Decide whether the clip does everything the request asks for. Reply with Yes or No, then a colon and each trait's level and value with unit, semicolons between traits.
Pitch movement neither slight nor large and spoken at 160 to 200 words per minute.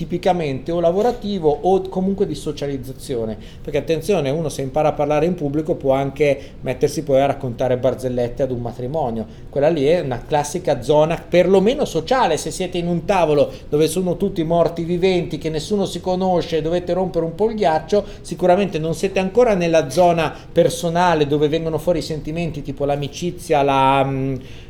Yes: average, 3.9 semitones; fast, 170 wpm